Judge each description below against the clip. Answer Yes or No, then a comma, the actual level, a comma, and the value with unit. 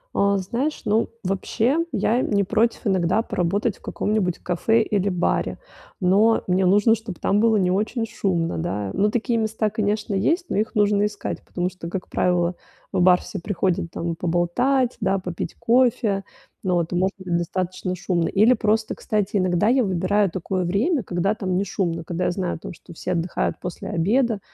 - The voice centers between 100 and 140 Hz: No, high, 195 Hz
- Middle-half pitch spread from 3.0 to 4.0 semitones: Yes, average, 3.3 semitones